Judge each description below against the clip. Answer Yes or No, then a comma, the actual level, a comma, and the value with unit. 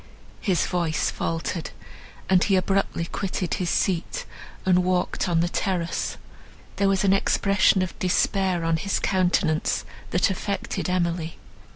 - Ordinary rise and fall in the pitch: No, narrow, 2.1 semitones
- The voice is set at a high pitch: No, medium, 180 Hz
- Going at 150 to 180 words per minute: No, slow, 135 wpm